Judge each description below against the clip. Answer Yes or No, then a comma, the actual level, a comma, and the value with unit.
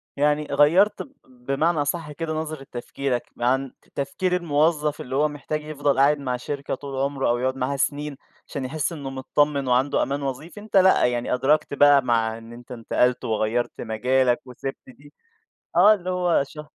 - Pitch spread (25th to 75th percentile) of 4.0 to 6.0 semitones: No, average, 3.1 semitones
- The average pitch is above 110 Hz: Yes, medium, 140 Hz